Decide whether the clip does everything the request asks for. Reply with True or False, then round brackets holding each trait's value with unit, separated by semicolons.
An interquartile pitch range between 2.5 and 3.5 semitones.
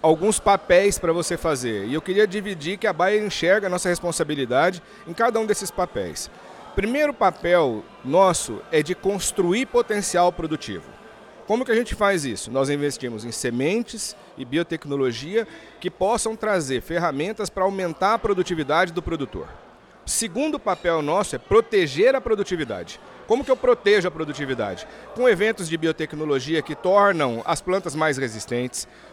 False (5.3 semitones)